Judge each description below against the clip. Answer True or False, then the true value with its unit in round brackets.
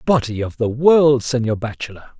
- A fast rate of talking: False (165 wpm)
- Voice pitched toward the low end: True (125 Hz)